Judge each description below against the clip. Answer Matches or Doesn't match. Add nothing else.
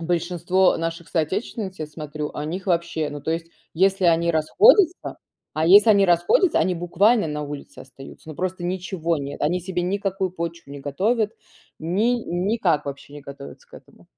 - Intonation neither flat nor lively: Matches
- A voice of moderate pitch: Matches